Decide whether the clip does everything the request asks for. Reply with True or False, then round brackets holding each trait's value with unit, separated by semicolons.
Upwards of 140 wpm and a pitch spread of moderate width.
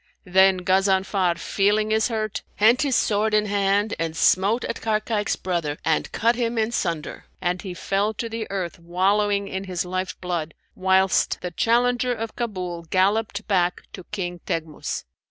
True (160 wpm; 3.2 semitones)